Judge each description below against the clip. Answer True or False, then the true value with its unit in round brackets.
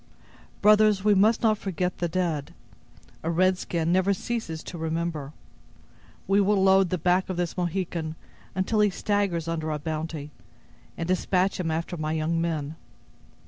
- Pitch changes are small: False (3.0 semitones)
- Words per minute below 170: True (155 wpm)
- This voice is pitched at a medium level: True (175 Hz)